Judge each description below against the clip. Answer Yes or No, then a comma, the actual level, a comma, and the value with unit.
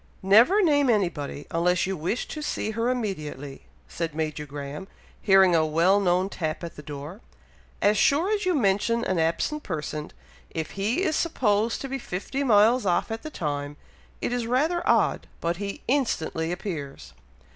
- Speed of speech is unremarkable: Yes, average, 165 wpm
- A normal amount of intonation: No, wide, 7.1 semitones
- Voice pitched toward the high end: Yes, high, 195 Hz